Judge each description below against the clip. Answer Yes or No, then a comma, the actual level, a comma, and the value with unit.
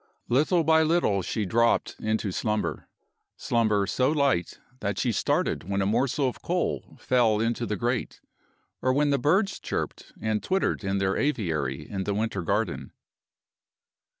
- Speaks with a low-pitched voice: Yes, low, 115 Hz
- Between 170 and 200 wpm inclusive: No, average, 150 wpm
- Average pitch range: No, wide, 5.7 semitones